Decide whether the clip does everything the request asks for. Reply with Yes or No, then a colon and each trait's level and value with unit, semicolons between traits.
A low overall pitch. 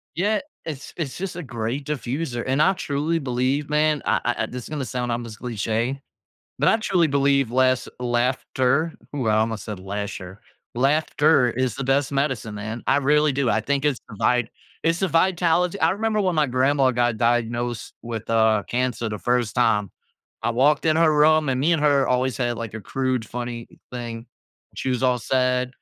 Yes: low, 130 Hz